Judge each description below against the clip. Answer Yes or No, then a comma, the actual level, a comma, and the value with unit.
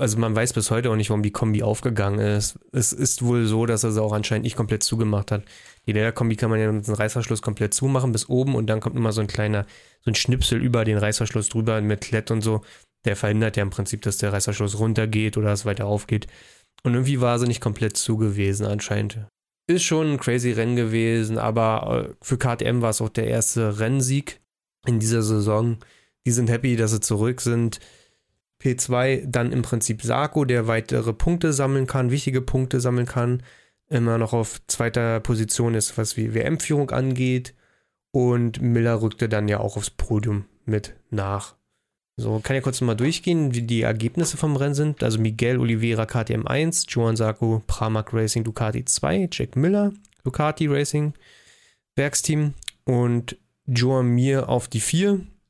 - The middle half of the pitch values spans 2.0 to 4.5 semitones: Yes, average, 2.7 semitones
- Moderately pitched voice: No, low, 115 Hz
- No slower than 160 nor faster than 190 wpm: Yes, average, 180 wpm